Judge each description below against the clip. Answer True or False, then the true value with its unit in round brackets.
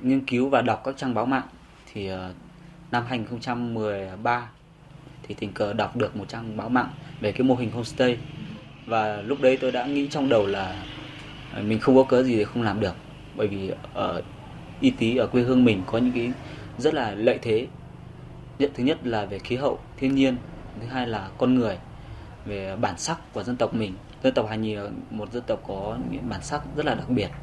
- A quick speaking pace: False (210 wpm)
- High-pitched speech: False (120 Hz)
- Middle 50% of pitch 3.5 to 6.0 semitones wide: True (3.9 semitones)